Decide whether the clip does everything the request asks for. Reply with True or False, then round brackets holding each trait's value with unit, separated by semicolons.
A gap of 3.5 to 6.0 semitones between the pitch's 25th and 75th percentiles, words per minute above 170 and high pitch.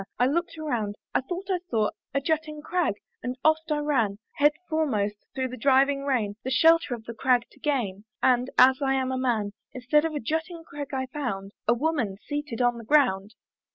True (4.4 semitones; 195 wpm; 265 Hz)